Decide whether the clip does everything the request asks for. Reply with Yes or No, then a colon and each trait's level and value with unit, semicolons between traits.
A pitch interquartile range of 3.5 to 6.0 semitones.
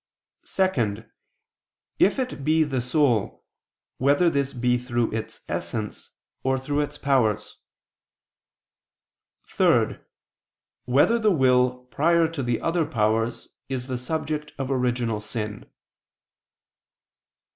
Yes: average, 4.1 semitones